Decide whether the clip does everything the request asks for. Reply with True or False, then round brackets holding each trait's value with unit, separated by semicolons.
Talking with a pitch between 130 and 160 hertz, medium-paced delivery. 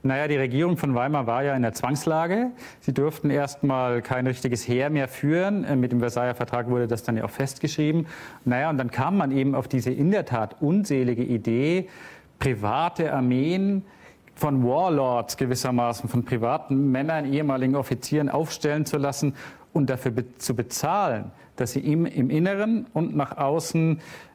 True (135 Hz; 165 wpm)